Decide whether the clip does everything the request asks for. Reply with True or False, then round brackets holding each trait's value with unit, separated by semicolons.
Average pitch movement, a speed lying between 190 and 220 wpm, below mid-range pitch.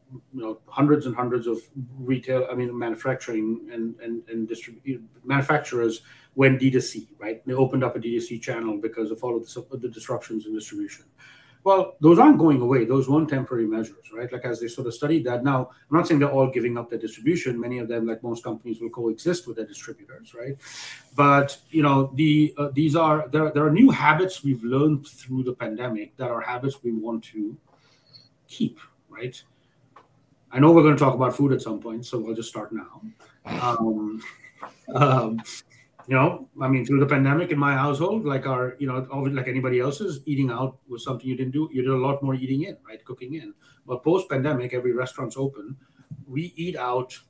True (3.0 semitones; 205 wpm; 130 Hz)